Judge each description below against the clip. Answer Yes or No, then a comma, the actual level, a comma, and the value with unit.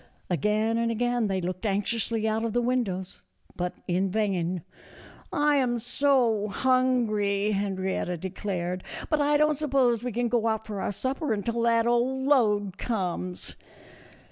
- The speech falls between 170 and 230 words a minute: No, average, 155 wpm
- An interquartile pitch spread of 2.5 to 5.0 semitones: Yes, average, 3.9 semitones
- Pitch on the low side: No, high, 220 Hz